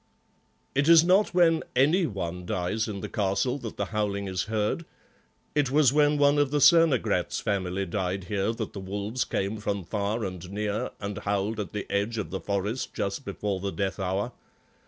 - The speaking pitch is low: Yes, low, 105 Hz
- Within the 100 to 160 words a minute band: No, average, 185 wpm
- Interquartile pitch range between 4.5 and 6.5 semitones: Yes, average, 5.2 semitones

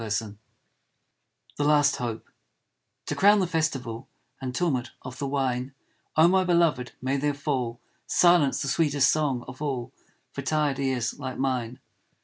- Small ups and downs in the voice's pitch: No, average, 3.3 semitones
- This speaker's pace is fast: No, average, 145 wpm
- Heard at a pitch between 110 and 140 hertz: Yes, low, 135 Hz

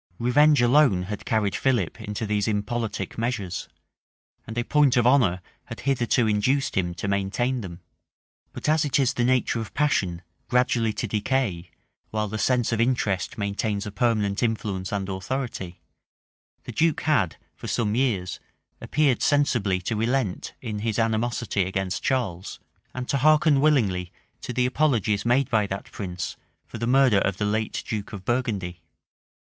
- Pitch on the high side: No, low, 110 Hz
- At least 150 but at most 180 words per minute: Yes, average, 160 wpm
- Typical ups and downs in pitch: Yes, average, 4.3 semitones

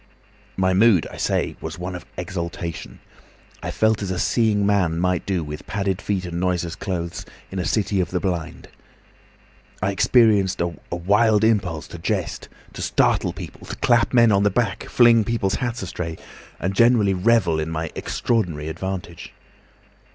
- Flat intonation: No, average, 3.4 semitones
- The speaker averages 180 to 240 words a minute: No, average, 165 wpm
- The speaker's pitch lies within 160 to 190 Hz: No, very low, 95 Hz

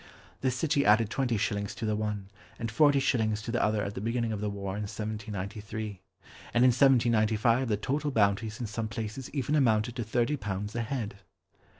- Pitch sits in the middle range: No, low, 110 Hz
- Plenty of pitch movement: No, average, 2.7 semitones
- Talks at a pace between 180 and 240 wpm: Yes, average, 195 wpm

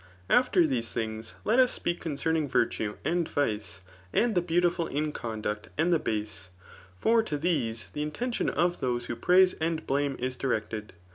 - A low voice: No, medium, 150 Hz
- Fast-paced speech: No, average, 165 wpm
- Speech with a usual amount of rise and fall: No, wide, 7.3 semitones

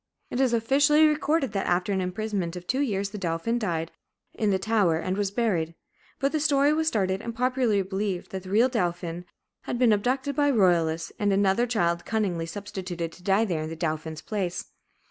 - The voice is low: No, high, 200 Hz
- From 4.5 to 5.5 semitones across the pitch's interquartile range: Yes, average, 5.2 semitones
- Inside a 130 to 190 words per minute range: No, average, 200 wpm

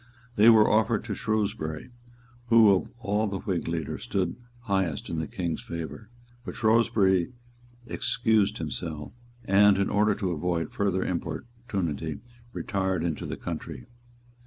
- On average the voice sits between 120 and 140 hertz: No, very low, 95 Hz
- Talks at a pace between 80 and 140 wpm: Yes, slow, 135 wpm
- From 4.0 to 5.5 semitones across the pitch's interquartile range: Yes, average, 4.4 semitones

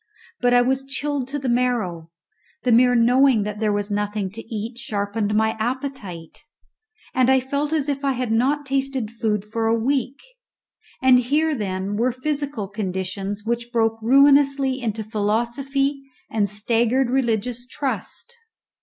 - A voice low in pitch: No, high, 240 Hz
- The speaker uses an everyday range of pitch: Yes, average, 4.2 semitones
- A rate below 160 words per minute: Yes, average, 150 wpm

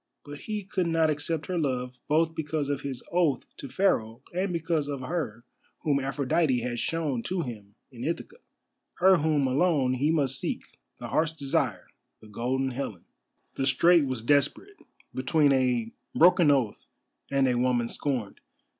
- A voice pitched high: No, medium, 140 Hz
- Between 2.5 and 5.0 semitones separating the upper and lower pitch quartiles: Yes, average, 4.4 semitones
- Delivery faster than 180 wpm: No, average, 160 wpm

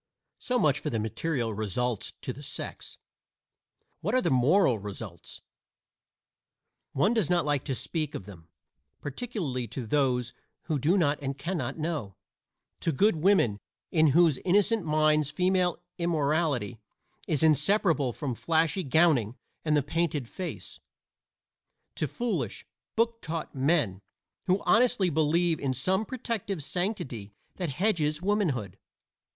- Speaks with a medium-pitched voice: Yes, medium, 155 Hz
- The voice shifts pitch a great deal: Yes, wide, 5.7 semitones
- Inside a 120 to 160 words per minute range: Yes, slow, 135 wpm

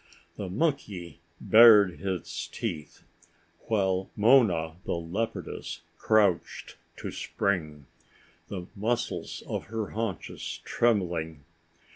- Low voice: Yes, very low, 95 Hz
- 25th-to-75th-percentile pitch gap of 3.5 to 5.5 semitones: Yes, average, 4.7 semitones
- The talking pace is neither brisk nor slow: No, slow, 90 wpm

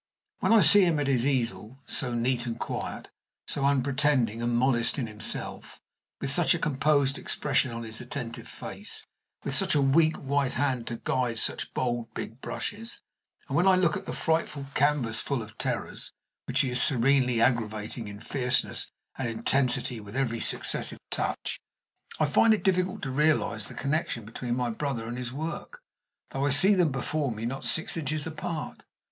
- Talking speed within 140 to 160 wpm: No, average, 175 wpm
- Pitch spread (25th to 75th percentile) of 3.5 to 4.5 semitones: Yes, average, 4.1 semitones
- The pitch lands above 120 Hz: Yes, low, 135 Hz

